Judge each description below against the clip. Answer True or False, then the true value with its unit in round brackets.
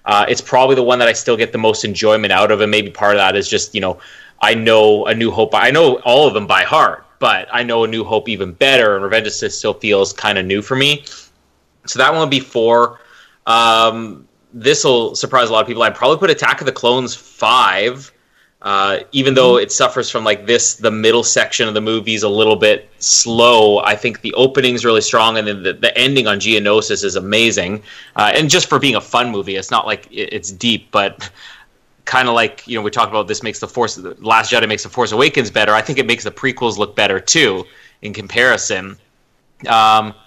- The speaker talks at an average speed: False (230 wpm)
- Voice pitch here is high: False (110 Hz)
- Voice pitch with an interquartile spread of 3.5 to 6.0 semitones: False (2.6 semitones)